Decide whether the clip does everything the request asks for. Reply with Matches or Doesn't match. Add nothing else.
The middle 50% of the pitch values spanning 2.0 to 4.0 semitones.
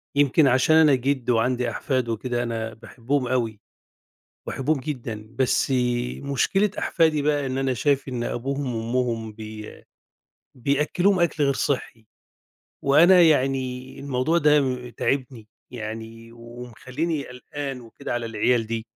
Matches